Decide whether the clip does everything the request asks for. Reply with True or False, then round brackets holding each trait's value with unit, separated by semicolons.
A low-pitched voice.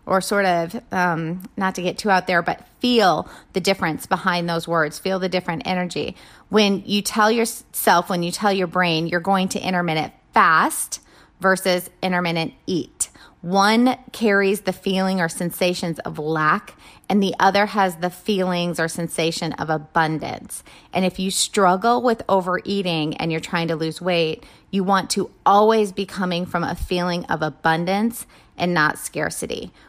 False (185 Hz)